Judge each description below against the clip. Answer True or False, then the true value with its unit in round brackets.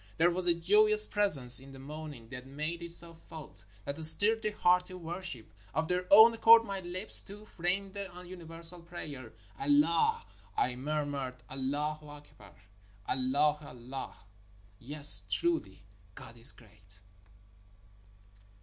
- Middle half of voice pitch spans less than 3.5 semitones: False (5.3 semitones)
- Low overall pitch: False (155 Hz)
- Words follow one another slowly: False (155 wpm)